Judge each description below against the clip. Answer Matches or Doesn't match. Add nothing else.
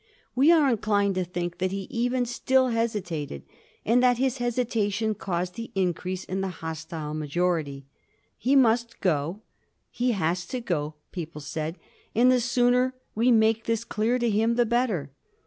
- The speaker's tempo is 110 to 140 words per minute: Doesn't match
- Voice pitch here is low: Doesn't match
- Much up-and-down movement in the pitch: Matches